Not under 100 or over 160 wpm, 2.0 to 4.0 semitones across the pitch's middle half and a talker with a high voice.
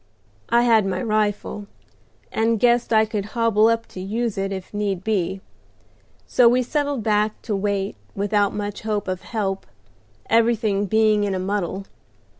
Yes: average, 155 wpm; narrow, 2.5 semitones; high, 210 Hz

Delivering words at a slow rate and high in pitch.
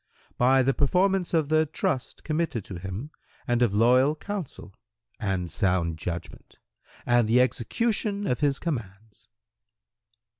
No: slow, 125 wpm; low, 125 Hz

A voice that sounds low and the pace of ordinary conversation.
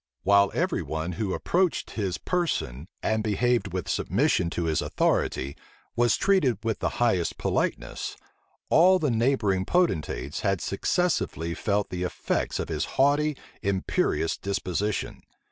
No: low, 105 Hz; slow, 130 wpm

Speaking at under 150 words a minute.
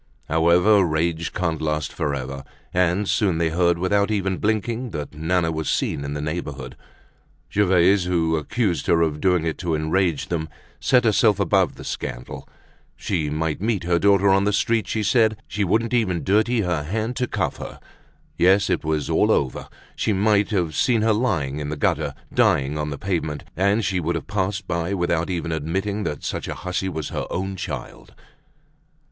No: average, 180 wpm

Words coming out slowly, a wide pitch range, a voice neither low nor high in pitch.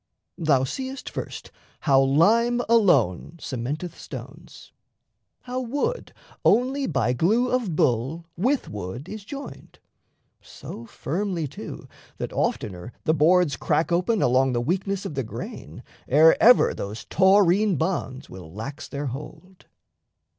Yes: slow, 125 wpm; wide, 8.1 semitones; medium, 165 Hz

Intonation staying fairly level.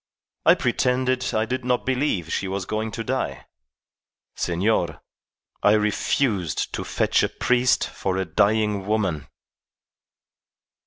No: average, 5.0 semitones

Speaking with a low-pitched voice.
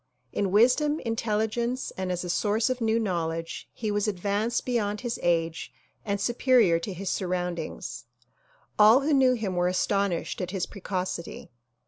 No: high, 205 Hz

